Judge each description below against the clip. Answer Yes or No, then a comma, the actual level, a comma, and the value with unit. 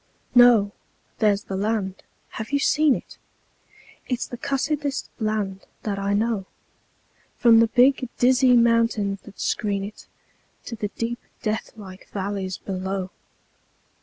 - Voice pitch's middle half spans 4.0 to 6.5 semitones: No, average, 3.5 semitones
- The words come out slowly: Yes, slow, 125 wpm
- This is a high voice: Yes, high, 215 Hz